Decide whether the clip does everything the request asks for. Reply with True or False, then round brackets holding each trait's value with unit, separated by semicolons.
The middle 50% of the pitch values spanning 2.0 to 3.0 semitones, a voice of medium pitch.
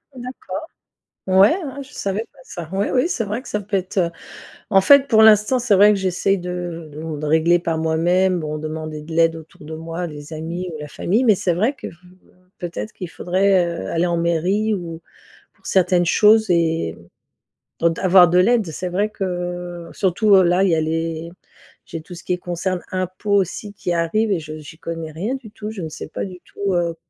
False (3.5 semitones; 180 Hz)